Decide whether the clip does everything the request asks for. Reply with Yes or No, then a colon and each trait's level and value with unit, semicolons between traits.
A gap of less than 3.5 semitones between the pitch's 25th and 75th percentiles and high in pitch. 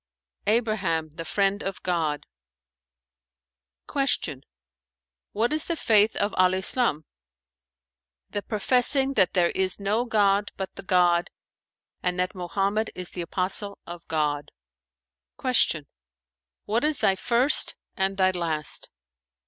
No: average, 3.8 semitones; high, 195 Hz